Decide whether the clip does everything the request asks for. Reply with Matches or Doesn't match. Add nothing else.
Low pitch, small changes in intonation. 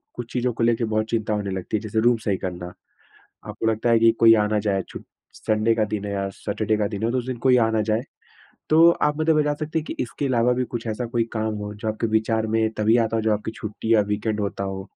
Matches